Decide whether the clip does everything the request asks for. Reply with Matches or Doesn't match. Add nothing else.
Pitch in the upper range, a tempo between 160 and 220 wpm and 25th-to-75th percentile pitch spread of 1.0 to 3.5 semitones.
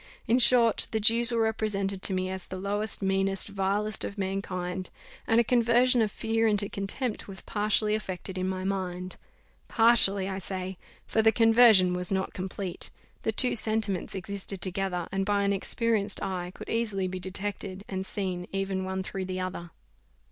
Matches